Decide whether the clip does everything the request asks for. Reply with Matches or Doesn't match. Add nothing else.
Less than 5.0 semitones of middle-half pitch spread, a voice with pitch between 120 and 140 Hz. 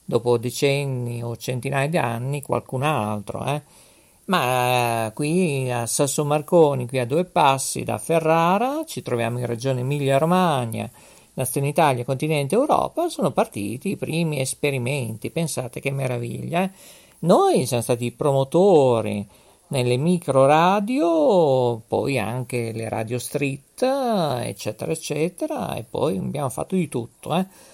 Doesn't match